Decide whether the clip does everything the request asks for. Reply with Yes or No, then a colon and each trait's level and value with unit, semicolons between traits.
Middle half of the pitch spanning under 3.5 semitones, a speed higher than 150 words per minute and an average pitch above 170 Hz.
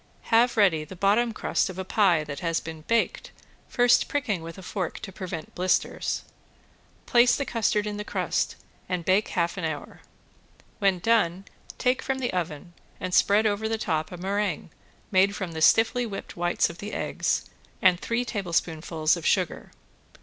No: average, 4.2 semitones; average, 170 wpm; high, 190 Hz